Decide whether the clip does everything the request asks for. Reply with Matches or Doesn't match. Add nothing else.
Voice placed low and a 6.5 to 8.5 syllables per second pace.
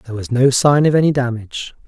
Matches